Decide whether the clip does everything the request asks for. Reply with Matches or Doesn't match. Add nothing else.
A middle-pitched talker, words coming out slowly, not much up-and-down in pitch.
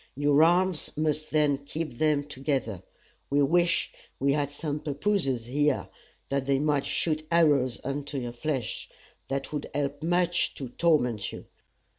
Doesn't match